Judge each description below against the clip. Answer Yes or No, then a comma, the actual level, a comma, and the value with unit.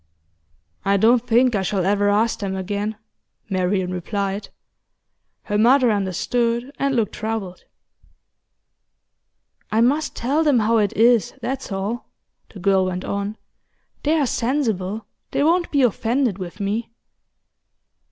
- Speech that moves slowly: Yes, slow, 130 wpm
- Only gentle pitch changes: No, average, 3.8 semitones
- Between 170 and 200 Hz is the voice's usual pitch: No, high, 215 Hz